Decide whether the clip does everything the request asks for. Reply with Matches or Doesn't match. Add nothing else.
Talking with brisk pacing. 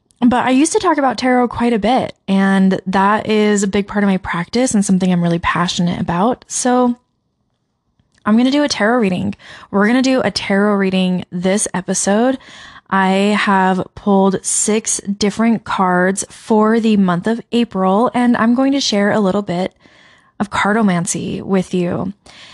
Doesn't match